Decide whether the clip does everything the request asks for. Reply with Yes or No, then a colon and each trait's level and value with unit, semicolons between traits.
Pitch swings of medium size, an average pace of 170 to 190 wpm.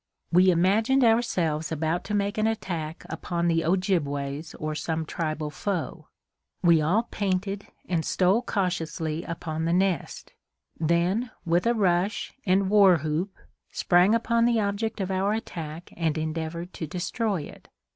No: average, 3.8 semitones; average, 145 wpm